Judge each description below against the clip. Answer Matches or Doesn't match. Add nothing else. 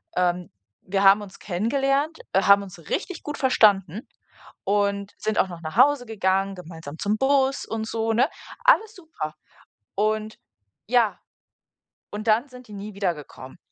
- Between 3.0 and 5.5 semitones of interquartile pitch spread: Matches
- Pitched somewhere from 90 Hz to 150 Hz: Doesn't match